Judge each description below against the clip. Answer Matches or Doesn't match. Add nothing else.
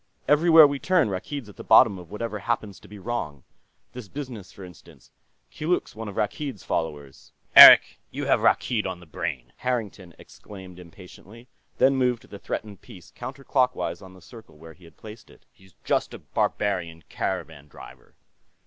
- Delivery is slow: Doesn't match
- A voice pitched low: Matches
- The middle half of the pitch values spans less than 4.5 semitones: Doesn't match